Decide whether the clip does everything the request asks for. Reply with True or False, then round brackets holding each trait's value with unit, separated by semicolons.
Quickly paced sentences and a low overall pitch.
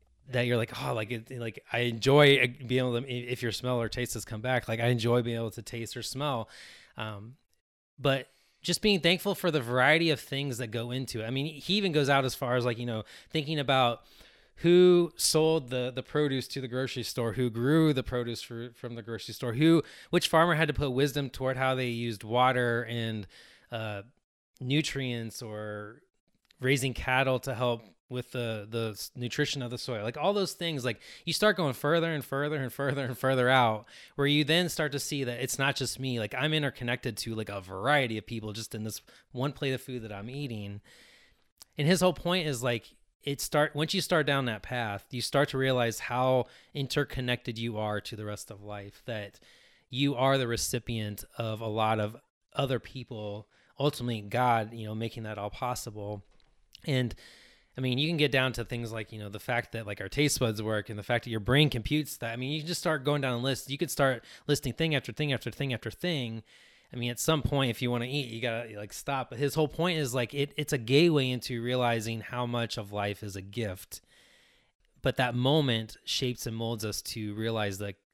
True (220 wpm; 125 Hz)